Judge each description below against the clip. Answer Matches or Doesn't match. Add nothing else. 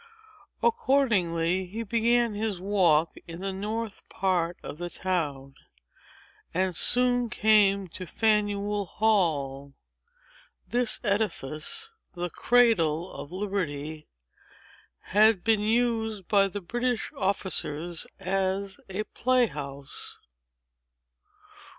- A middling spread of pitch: Matches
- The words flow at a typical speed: Doesn't match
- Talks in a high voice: Matches